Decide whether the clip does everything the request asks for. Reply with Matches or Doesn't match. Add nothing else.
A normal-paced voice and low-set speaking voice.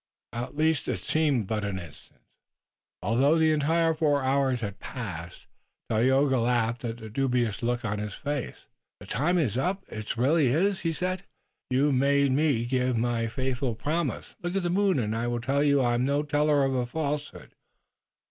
Matches